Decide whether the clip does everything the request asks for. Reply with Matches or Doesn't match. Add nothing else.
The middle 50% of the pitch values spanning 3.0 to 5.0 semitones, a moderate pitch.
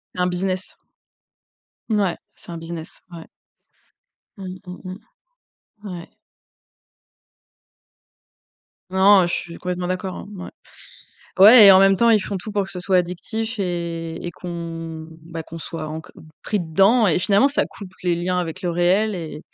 Doesn't match